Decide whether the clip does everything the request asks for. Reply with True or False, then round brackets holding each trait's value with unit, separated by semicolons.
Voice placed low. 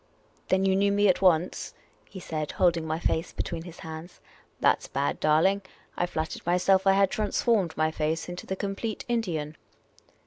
False (175 Hz)